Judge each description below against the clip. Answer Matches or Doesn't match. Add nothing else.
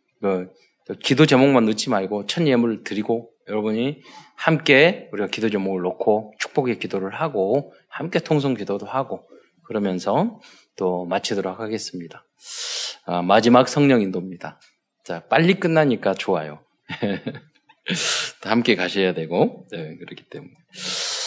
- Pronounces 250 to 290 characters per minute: Matches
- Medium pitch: Doesn't match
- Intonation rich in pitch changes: Matches